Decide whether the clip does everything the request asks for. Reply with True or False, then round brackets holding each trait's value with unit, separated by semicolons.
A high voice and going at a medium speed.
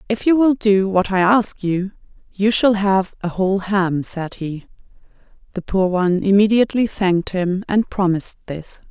True (195 Hz; 170 wpm)